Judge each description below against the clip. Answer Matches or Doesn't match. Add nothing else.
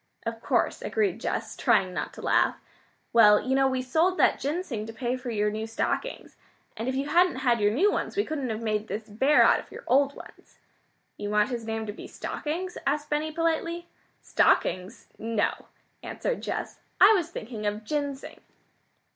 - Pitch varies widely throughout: Matches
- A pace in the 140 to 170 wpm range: Doesn't match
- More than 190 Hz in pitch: Matches